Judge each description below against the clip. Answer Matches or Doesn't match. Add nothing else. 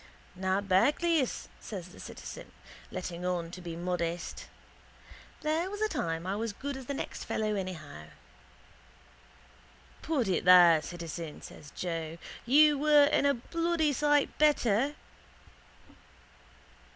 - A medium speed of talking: Doesn't match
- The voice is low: Doesn't match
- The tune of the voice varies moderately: Doesn't match